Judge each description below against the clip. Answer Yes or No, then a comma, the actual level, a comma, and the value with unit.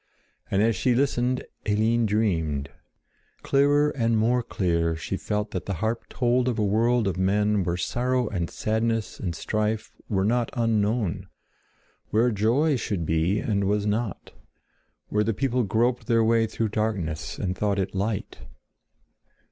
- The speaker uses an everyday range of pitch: Yes, average, 3.2 semitones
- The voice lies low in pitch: Yes, low, 110 Hz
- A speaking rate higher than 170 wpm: No, average, 150 wpm